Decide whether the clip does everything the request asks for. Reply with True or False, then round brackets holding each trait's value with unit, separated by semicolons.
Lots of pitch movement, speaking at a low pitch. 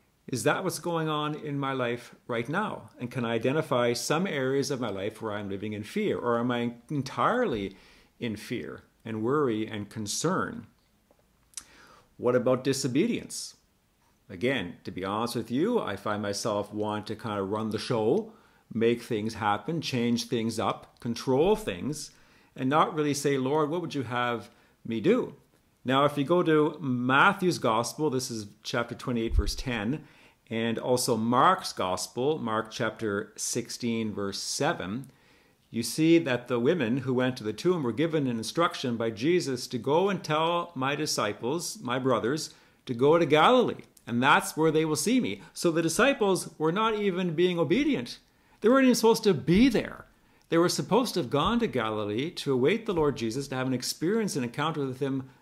True (5.7 semitones; 130 Hz)